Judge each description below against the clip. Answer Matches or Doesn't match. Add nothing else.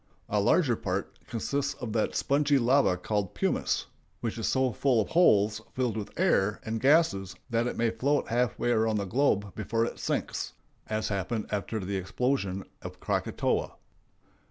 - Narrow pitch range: Doesn't match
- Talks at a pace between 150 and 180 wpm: Matches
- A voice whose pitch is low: Matches